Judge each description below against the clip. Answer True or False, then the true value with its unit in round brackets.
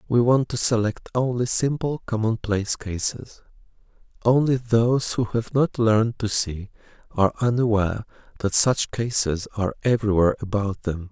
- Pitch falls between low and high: False (110 Hz)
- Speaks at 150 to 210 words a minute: False (135 wpm)